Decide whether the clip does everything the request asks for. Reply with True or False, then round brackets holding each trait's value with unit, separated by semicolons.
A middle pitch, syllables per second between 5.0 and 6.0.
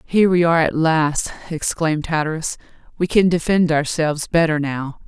True (160 Hz; 5.3 syllables/s)